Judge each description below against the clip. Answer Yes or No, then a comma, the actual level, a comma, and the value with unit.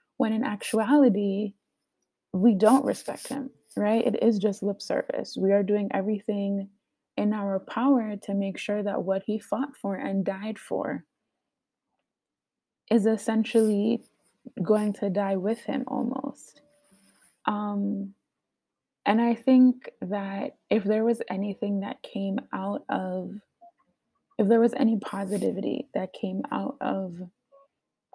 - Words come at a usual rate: No, slow, 130 wpm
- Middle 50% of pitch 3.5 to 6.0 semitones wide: No, average, 2.7 semitones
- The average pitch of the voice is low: No, high, 215 Hz